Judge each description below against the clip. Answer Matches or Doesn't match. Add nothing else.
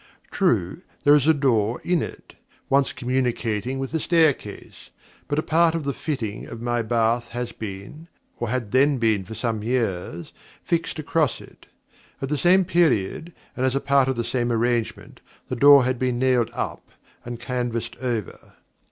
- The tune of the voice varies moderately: Matches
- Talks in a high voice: Doesn't match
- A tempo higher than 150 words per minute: Matches